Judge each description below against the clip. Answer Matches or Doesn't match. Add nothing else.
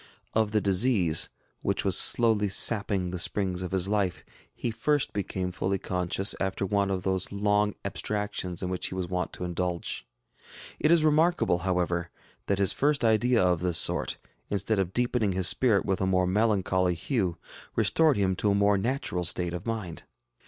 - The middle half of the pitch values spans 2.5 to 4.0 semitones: Matches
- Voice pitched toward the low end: Matches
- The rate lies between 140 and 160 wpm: Doesn't match